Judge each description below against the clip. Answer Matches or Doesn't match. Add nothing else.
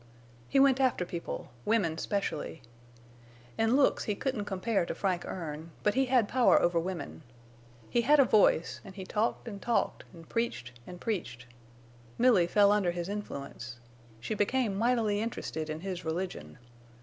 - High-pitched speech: Matches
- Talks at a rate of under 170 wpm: Matches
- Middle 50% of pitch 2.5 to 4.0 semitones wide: Doesn't match